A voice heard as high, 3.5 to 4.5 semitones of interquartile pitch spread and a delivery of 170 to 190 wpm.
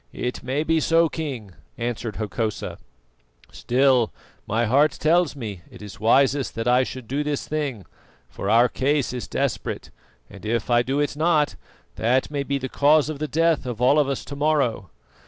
No: low, 130 Hz; average, 4.1 semitones; average, 180 wpm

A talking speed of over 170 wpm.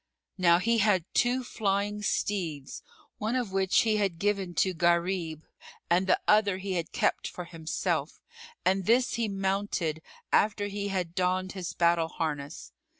No: average, 150 wpm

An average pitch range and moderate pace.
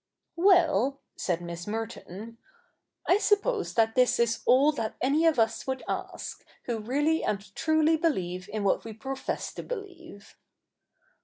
No: wide, 6.9 semitones; average, 145 wpm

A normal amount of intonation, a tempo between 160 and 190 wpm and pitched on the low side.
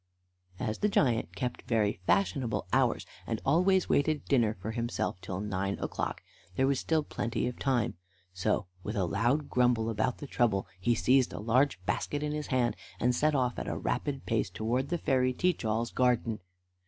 Yes: average, 3.9 semitones; average, 180 wpm; low, 120 Hz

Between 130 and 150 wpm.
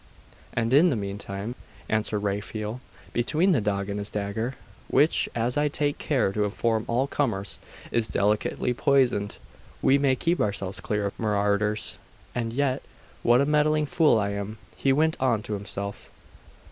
No: average, 160 wpm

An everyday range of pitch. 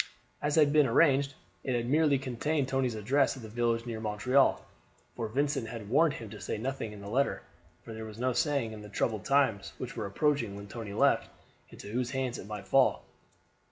Yes: average, 4.1 semitones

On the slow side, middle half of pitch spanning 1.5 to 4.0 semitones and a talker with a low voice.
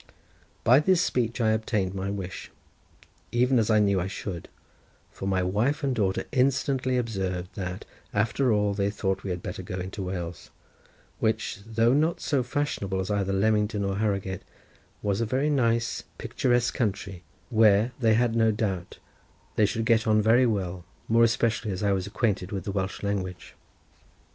No: average, 170 wpm; average, 3.4 semitones; low, 105 Hz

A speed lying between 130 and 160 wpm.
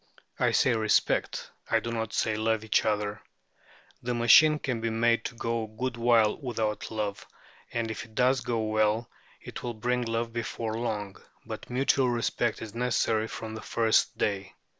No: average, 170 wpm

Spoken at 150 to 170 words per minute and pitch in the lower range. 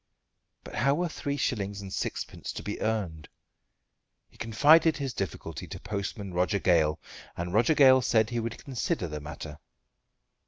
Yes: average, 155 wpm; low, 105 Hz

